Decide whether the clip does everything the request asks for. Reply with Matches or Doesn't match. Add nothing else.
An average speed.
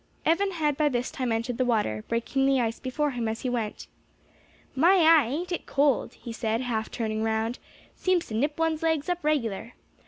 Matches